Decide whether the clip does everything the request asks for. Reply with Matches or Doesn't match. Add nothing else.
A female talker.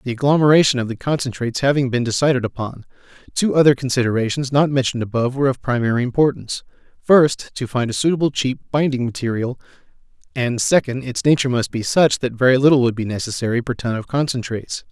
Doesn't match